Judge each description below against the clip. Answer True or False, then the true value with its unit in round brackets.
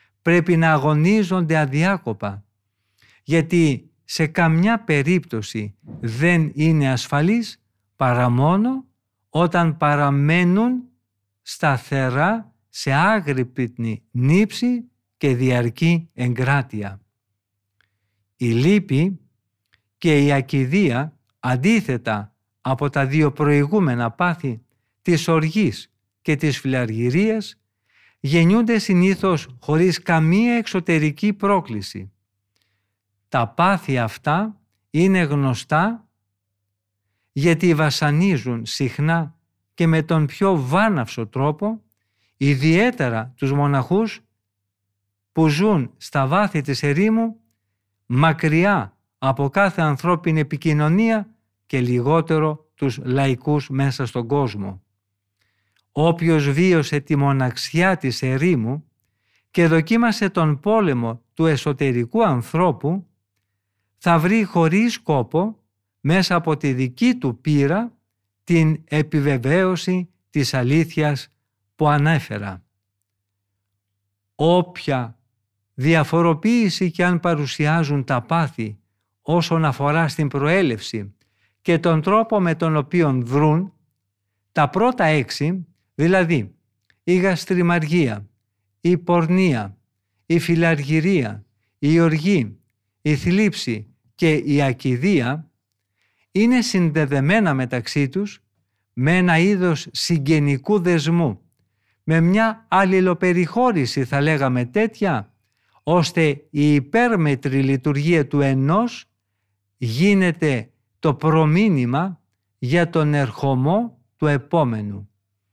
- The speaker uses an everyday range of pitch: False (7.2 semitones)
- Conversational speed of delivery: False (90 wpm)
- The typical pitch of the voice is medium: True (145 Hz)